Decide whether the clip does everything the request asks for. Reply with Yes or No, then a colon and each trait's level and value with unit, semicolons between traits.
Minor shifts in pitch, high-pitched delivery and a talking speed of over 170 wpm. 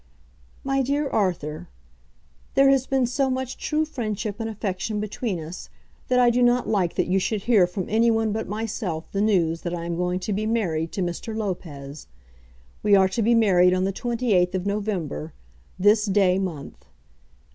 No: average, 4.4 semitones; high, 205 Hz; average, 180 wpm